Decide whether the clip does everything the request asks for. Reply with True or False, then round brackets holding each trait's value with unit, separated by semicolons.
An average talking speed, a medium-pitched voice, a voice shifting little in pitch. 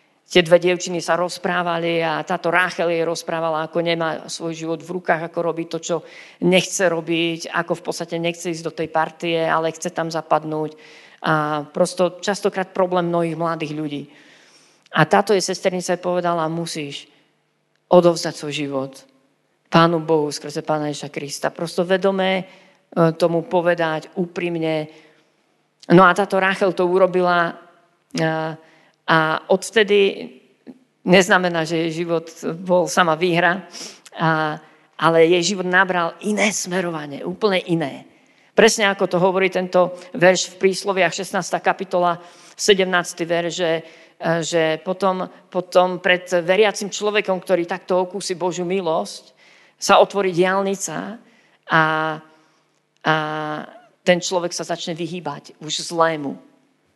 True (125 wpm; 170 Hz; 2.3 semitones)